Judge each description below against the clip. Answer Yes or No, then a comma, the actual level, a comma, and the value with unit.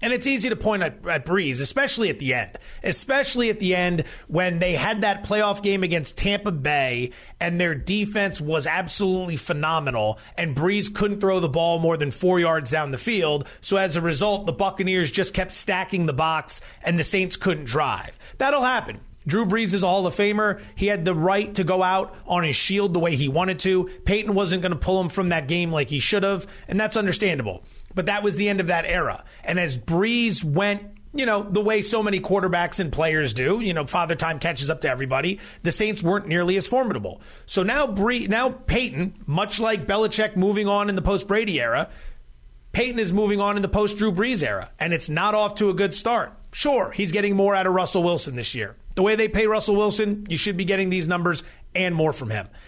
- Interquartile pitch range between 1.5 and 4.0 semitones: Yes, average, 3.6 semitones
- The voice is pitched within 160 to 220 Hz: Yes, high, 190 Hz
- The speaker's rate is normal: No, fast, 220 wpm